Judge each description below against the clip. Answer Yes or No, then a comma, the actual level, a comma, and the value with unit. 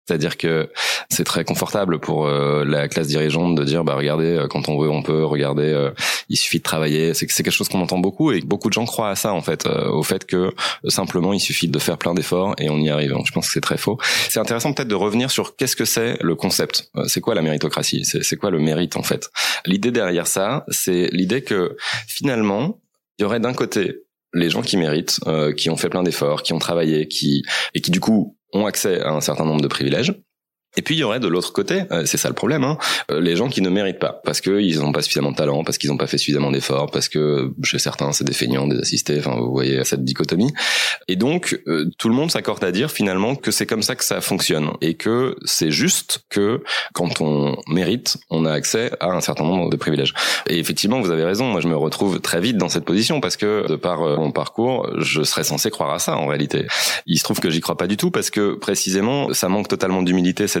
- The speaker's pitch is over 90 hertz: No, very low, 75 Hz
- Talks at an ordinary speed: No, fast, 245 wpm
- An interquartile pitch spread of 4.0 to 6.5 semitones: No, average, 2.7 semitones